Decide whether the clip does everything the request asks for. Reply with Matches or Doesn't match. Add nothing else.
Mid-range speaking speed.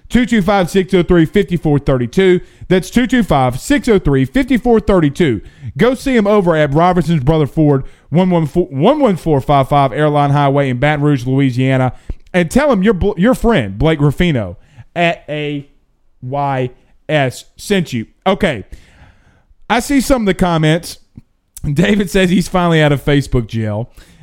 Doesn't match